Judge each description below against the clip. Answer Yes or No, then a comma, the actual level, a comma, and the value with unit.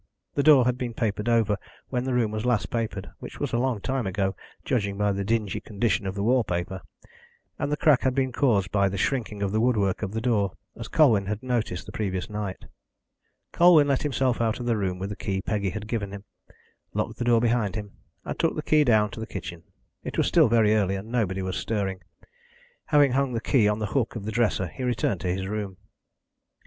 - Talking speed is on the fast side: Yes, fast, 225 wpm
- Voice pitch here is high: No, low, 110 Hz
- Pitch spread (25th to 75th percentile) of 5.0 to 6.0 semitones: No, average, 3.8 semitones